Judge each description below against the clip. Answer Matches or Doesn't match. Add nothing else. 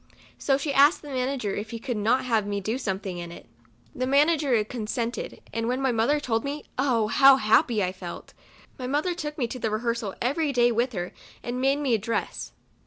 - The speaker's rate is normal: Doesn't match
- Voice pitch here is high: Matches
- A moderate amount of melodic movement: Matches